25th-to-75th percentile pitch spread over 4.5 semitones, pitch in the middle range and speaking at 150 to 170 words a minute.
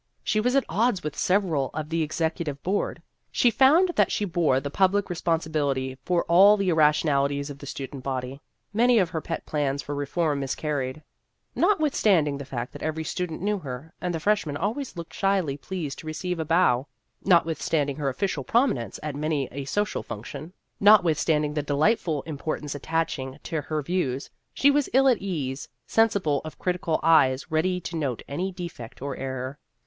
No: average, 4.9 semitones; medium, 160 Hz; average, 185 wpm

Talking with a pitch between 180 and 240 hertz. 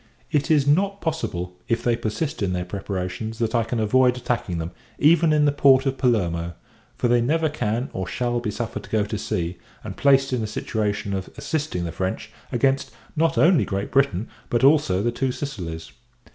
No: low, 120 Hz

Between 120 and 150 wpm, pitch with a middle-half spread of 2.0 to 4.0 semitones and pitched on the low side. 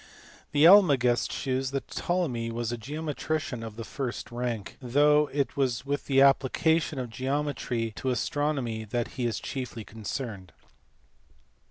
Yes: average, 140 wpm; average, 3.6 semitones; low, 130 Hz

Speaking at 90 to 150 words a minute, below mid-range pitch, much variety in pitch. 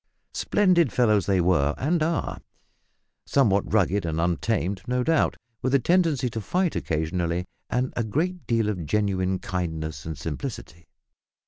Yes: average, 140 wpm; low, 105 Hz; wide, 7.5 semitones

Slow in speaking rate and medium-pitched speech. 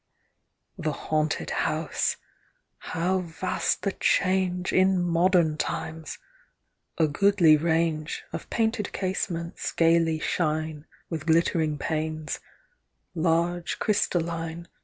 Yes: slow, 95 wpm; medium, 165 Hz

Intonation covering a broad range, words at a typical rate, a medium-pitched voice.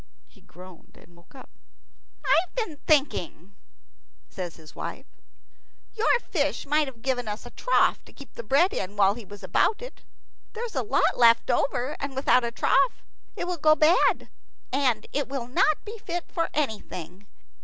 No: wide, 7.0 semitones; average, 165 wpm; very high, 270 Hz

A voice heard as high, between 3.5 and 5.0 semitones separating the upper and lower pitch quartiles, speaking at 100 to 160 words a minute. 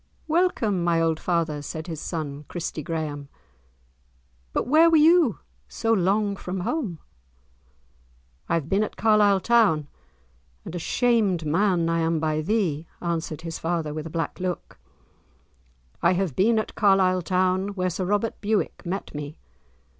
No: medium, 180 Hz; average, 4.2 semitones; average, 150 wpm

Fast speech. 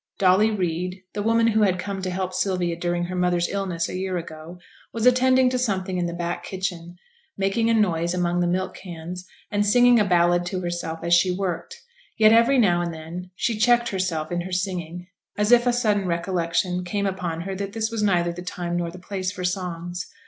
Yes: fast, 210 wpm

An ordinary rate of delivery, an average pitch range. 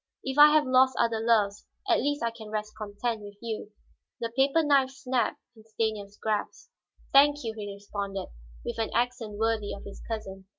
Yes: average, 180 wpm; average, 3.9 semitones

